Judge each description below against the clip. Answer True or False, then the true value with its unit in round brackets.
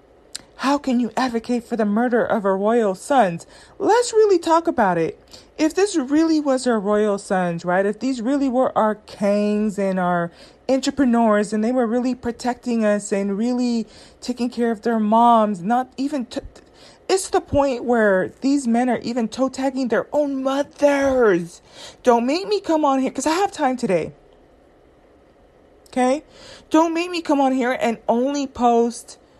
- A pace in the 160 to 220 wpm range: True (170 wpm)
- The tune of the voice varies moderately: True (4.1 semitones)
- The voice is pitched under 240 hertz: False (245 Hz)